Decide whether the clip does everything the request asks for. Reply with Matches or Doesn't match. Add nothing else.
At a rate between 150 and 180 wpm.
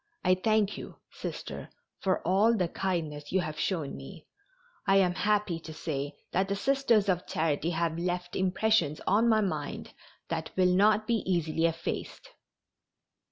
Matches